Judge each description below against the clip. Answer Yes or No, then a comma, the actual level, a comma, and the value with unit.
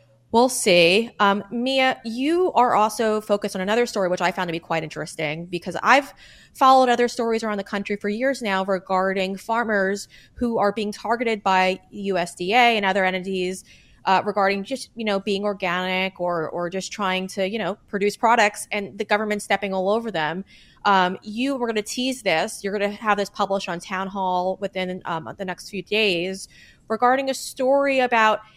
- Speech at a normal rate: Yes, average, 185 wpm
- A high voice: Yes, high, 205 Hz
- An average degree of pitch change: Yes, average, 3.3 semitones